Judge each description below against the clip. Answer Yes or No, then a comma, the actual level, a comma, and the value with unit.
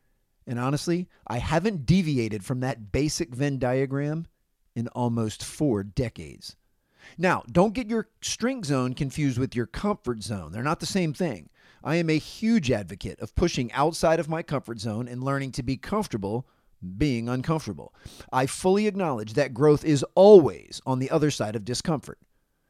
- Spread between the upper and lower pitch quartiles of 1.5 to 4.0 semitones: No, average, 5.1 semitones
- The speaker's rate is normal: Yes, average, 165 wpm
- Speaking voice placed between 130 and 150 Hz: Yes, medium, 140 Hz